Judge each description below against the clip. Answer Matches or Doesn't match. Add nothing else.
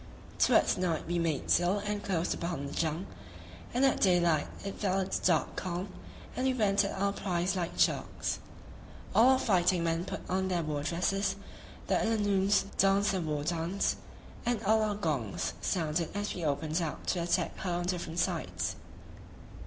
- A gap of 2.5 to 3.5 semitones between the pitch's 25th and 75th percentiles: Matches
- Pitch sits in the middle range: Matches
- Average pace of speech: Matches